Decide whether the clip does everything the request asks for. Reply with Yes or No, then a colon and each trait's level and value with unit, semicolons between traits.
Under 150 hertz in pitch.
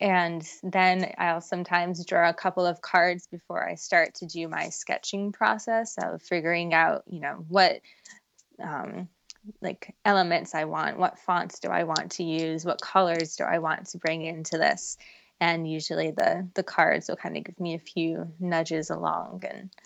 No: medium, 175 Hz